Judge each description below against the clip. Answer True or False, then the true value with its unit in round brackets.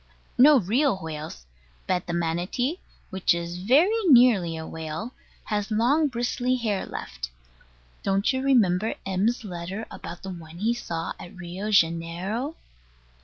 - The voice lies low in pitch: False (195 Hz)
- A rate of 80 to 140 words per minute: True (135 wpm)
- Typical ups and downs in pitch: False (6.1 semitones)